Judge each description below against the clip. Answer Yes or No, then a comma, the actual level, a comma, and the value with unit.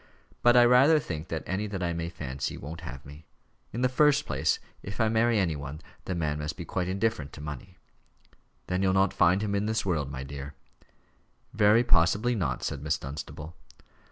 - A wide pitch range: Yes, wide, 6.5 semitones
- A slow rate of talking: No, average, 195 wpm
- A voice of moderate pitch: No, very low, 90 Hz